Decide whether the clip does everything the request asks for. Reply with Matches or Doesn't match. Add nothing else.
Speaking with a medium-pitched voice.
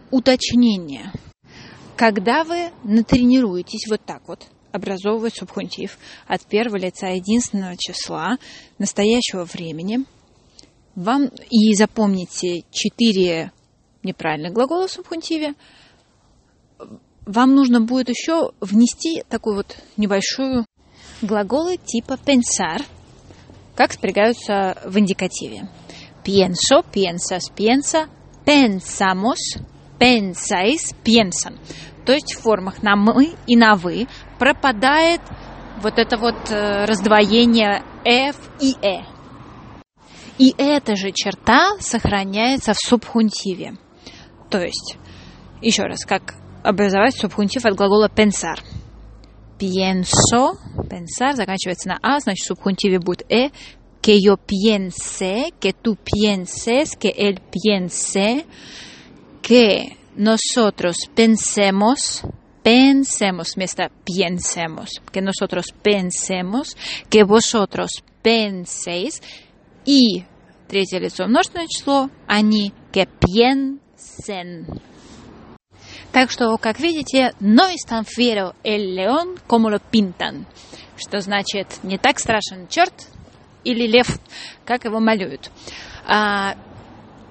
Doesn't match